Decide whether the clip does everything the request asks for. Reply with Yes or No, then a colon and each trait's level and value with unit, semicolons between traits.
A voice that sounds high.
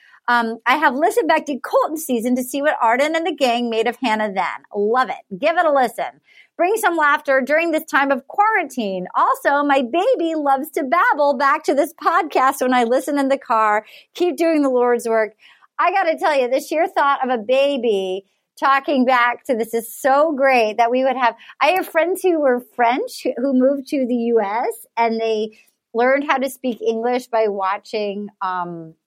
Yes: very high, 265 Hz